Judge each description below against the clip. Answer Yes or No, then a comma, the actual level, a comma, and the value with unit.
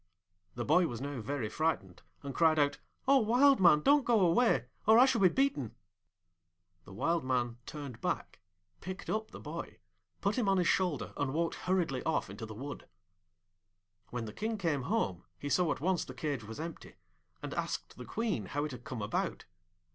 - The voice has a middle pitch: Yes, medium, 155 Hz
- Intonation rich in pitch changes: Yes, wide, 7.4 semitones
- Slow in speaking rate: No, average, 190 wpm